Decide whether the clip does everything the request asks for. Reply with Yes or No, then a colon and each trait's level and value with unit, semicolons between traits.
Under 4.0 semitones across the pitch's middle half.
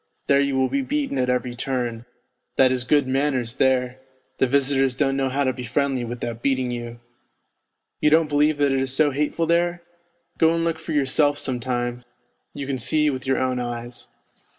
Yes: average, 2.7 semitones